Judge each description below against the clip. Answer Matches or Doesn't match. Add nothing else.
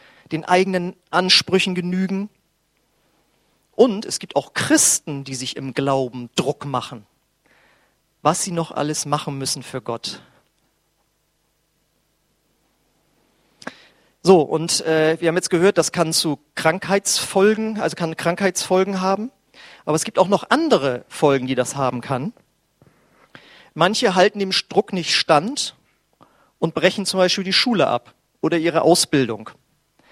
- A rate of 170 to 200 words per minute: Doesn't match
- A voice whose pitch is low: Doesn't match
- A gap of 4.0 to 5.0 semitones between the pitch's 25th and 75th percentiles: Matches